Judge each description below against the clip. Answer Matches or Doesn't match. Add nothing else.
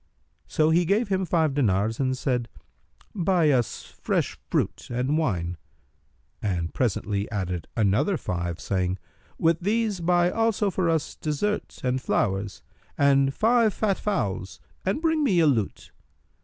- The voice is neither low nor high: Matches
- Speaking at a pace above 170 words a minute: Doesn't match